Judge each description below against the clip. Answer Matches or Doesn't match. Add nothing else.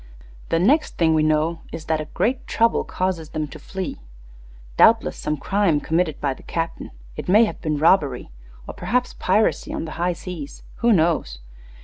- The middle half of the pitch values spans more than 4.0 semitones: Doesn't match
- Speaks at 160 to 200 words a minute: Matches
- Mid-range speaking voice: Matches